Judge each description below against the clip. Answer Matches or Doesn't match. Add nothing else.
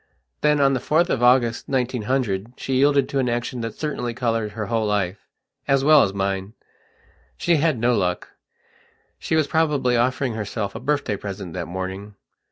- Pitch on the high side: Doesn't match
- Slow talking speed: Doesn't match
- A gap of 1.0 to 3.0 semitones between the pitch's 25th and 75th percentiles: Doesn't match